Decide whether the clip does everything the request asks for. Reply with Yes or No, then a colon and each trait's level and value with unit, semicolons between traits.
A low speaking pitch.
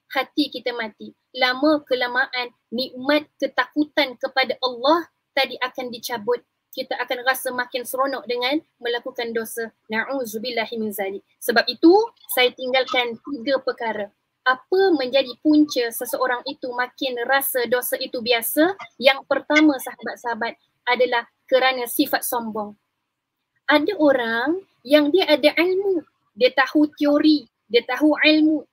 No: very high, 260 Hz